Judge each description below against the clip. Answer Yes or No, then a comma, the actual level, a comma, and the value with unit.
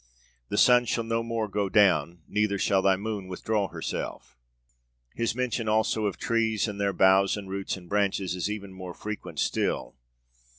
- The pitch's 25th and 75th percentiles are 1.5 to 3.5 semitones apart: Yes, narrow, 2.5 semitones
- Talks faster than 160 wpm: Yes, average, 170 wpm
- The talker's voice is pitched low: Yes, low, 100 Hz